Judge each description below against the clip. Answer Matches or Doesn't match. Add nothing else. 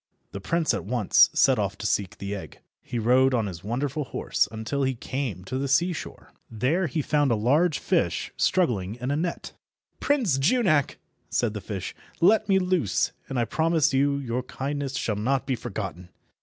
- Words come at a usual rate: Matches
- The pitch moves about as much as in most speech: Doesn't match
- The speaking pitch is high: Doesn't match